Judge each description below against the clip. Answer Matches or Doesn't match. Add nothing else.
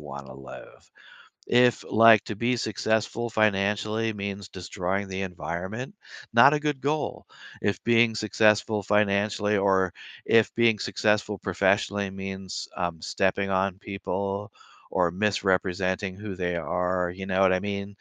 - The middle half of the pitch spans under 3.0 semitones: Matches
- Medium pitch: Doesn't match